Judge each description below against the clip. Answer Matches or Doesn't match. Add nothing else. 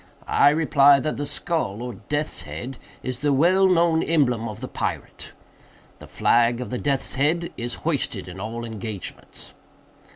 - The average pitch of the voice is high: Doesn't match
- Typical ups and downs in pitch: Matches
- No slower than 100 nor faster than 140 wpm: Doesn't match